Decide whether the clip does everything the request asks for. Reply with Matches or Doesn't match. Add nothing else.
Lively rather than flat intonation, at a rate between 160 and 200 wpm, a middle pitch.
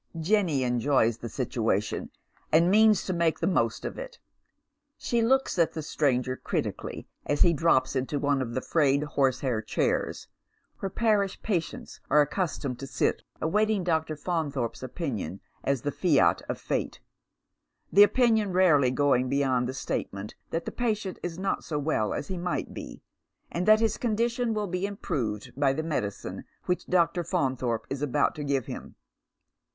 Matches